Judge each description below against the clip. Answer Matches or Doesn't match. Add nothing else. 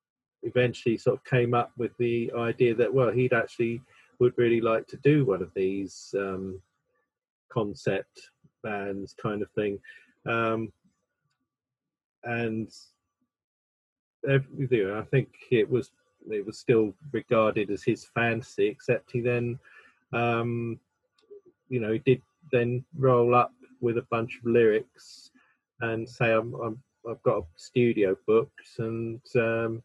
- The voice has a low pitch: Matches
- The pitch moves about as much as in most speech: Doesn't match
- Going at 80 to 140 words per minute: Matches